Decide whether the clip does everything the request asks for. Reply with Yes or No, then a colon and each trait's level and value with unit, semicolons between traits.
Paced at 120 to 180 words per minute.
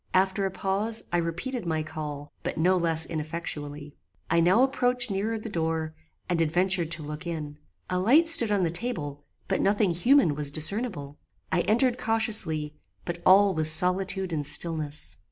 Yes: average, 165 wpm